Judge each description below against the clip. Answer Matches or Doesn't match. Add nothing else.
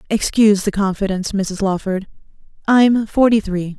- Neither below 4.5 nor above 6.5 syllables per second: Matches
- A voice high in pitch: Matches